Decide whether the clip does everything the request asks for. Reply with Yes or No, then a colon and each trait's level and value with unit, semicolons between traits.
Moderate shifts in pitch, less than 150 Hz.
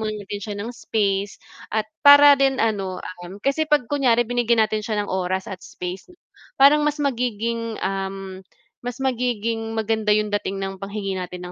No: average, 3.9 semitones; high, 215 Hz